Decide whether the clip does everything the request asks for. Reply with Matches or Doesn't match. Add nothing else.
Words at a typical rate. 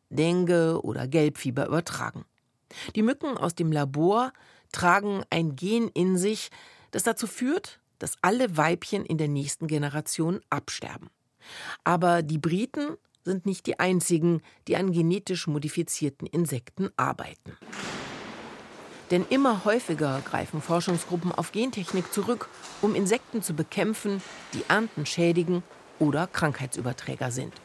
Doesn't match